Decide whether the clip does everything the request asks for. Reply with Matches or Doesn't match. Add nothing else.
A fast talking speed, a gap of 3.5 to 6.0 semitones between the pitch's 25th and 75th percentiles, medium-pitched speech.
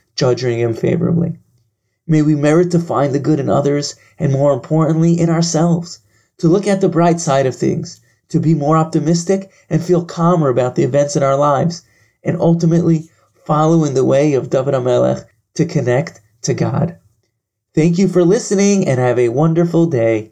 Doesn't match